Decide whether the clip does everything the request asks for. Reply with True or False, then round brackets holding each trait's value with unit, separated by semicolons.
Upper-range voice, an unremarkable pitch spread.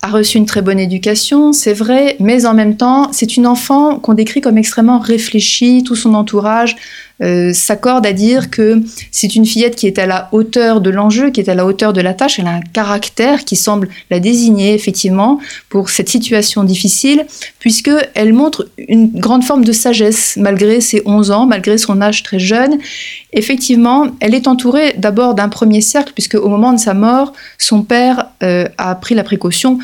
True (220 Hz; 3.3 semitones)